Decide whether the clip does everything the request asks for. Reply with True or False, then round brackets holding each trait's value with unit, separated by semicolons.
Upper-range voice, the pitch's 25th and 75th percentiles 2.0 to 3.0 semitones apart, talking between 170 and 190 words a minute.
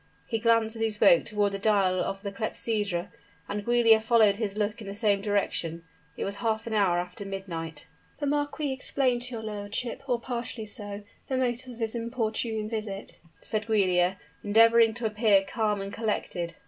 True (215 Hz; 2.6 semitones; 180 wpm)